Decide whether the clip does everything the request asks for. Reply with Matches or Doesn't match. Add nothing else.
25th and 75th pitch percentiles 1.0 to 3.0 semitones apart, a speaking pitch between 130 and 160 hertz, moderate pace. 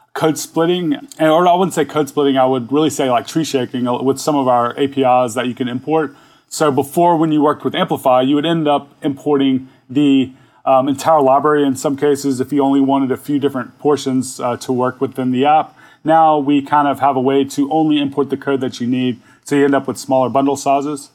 Doesn't match